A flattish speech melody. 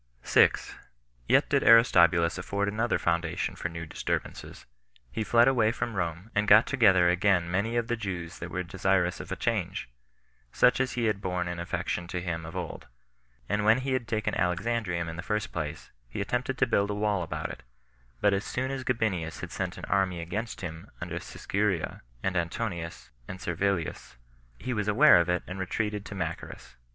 No: average, 4.1 semitones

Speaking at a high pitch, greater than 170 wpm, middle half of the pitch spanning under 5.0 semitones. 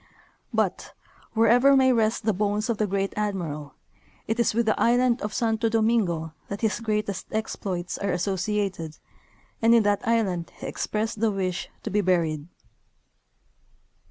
No: high, 210 Hz; average, 150 wpm; average, 3.4 semitones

